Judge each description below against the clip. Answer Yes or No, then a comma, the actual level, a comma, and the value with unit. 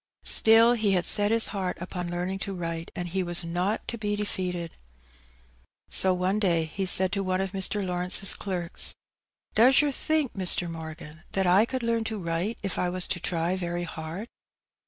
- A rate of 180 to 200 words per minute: Yes, average, 190 wpm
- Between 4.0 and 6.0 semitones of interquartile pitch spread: No, average, 2.9 semitones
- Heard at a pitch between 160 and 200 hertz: Yes, medium, 185 Hz